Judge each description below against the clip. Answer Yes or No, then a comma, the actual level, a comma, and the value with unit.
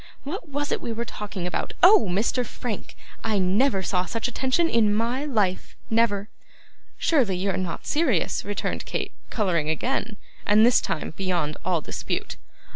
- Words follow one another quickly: No, average, 160 wpm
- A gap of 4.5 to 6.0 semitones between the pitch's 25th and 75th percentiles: Yes, average, 5.1 semitones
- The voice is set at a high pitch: Yes, high, 215 Hz